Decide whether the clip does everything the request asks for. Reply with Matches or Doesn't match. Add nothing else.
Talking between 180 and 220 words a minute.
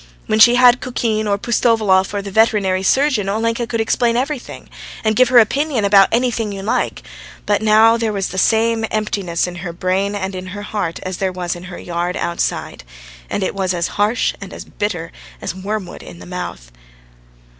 Matches